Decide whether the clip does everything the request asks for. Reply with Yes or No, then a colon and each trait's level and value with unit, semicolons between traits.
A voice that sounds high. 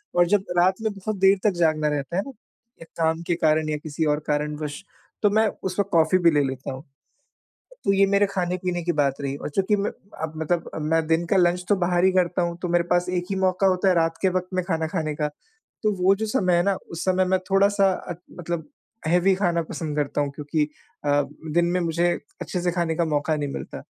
No: medium, 175 Hz